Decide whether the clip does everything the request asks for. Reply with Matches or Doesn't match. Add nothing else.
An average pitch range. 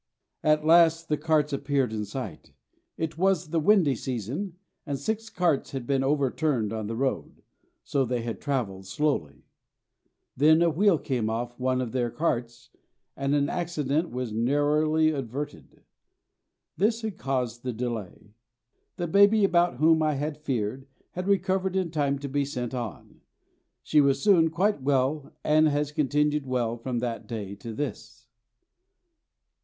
Matches